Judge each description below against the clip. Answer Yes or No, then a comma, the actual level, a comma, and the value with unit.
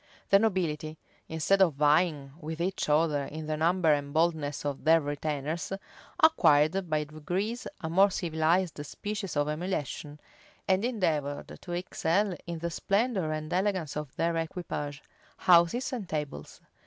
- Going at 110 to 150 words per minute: Yes, average, 140 wpm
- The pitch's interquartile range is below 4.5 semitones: Yes, average, 3.7 semitones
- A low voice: No, medium, 160 Hz